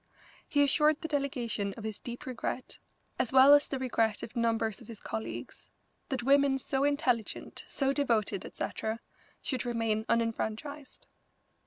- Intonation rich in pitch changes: No, average, 4.0 semitones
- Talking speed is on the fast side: No, average, 145 wpm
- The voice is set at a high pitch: Yes, high, 245 Hz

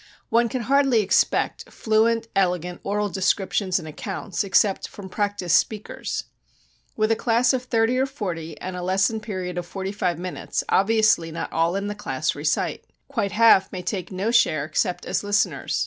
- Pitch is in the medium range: No, high, 200 Hz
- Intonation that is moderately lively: Yes, average, 3.8 semitones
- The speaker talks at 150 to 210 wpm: Yes, average, 170 wpm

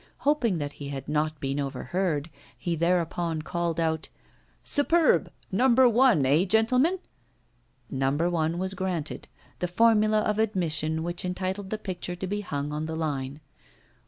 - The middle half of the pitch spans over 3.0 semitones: Yes, average, 5.1 semitones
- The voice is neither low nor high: Yes, medium, 175 Hz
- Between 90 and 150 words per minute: Yes, average, 145 wpm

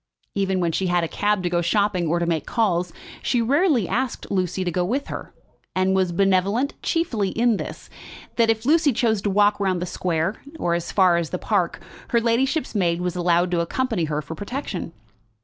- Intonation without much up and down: No, average, 4.7 semitones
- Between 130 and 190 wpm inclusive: No, average, 200 wpm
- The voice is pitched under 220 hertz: Yes, high, 190 Hz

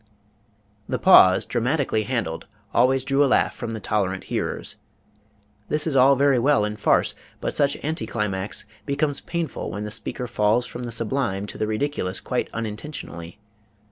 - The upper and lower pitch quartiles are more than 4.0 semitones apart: Yes, average, 4.9 semitones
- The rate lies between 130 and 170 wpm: Yes, average, 160 wpm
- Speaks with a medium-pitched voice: No, low, 120 Hz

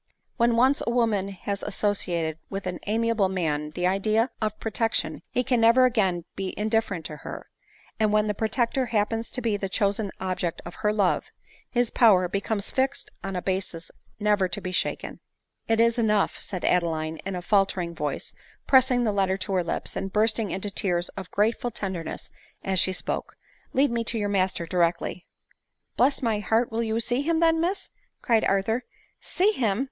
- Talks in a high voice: Yes, high, 205 Hz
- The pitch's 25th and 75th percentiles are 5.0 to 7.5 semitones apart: No, average, 3.7 semitones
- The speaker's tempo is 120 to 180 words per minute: No, average, 190 wpm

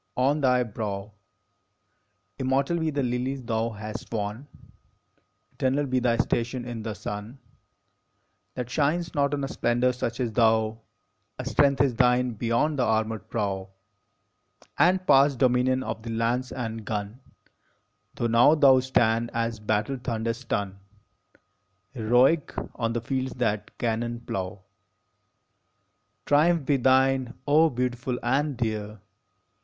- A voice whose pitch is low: Yes, low, 120 Hz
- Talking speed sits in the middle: No, slow, 130 wpm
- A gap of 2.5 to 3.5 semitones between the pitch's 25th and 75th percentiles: Yes, average, 3.0 semitones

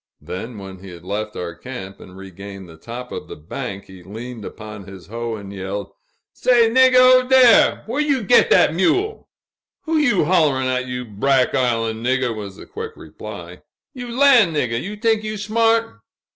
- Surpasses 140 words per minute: Yes, average, 180 wpm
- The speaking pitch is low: Yes, low, 125 Hz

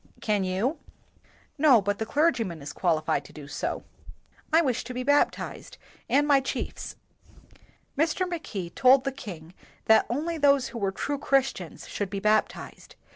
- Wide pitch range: Yes, wide, 6.7 semitones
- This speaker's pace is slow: No, average, 160 wpm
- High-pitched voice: Yes, high, 245 Hz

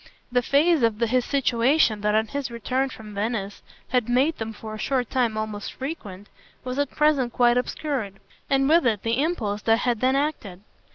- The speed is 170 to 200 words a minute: Yes, average, 185 wpm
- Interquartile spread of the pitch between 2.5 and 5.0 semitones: Yes, average, 4.0 semitones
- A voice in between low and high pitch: No, high, 245 Hz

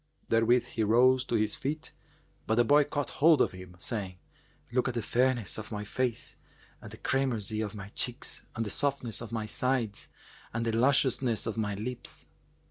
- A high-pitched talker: No, low, 115 Hz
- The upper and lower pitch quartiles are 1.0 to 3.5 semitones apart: Yes, average, 3.1 semitones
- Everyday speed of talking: Yes, average, 185 wpm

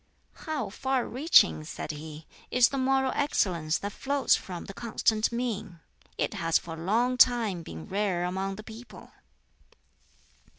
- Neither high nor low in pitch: No, high, 210 Hz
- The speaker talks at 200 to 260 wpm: No, average, 145 wpm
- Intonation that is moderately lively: No, wide, 6.6 semitones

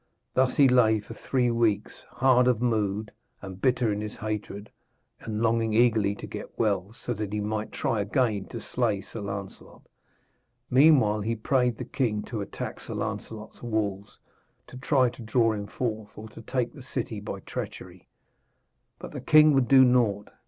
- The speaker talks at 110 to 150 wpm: No, average, 170 wpm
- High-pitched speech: No, low, 110 Hz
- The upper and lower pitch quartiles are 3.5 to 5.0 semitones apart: No, average, 3.1 semitones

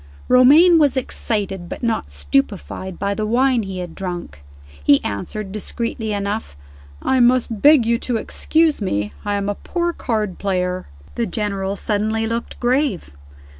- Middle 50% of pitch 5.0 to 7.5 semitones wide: No, average, 4.2 semitones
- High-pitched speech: Yes, high, 215 Hz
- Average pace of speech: Yes, average, 150 wpm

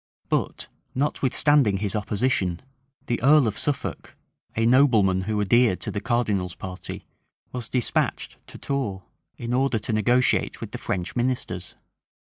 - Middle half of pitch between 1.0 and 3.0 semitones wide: No, average, 4.4 semitones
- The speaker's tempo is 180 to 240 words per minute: No, slow, 135 wpm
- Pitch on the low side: Yes, low, 115 Hz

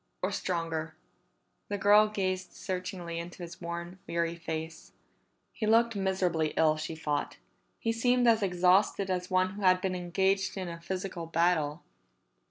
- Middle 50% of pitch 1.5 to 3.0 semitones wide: Yes, narrow, 2.5 semitones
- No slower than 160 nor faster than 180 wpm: No, average, 150 wpm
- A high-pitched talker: No, medium, 180 Hz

